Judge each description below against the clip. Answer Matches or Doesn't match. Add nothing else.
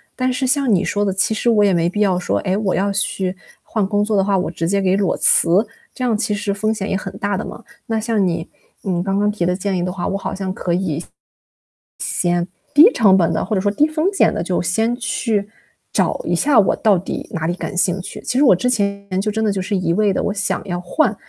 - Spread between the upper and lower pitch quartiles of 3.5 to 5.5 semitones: Doesn't match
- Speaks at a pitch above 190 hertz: Matches